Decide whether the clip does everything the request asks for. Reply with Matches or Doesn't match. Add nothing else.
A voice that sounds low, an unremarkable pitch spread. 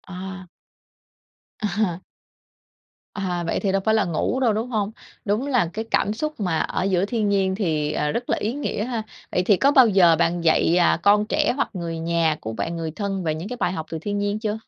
Doesn't match